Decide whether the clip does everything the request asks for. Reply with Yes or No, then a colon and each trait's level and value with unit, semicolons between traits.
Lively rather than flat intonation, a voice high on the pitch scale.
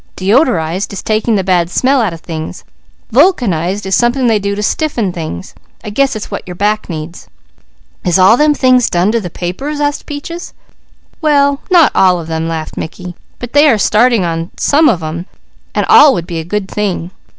Yes: wide, 7.0 semitones; high, 205 Hz